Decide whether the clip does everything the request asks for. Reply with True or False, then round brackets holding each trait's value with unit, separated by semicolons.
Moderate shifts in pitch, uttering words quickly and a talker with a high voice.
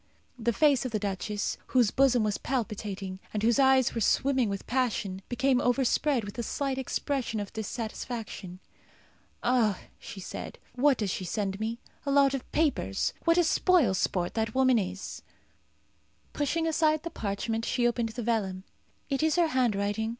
False (4.6 semitones; 165 wpm; 235 Hz)